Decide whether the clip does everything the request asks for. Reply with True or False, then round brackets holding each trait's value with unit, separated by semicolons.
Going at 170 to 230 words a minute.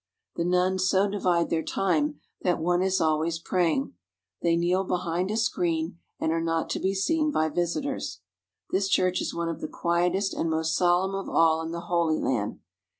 True (185 wpm)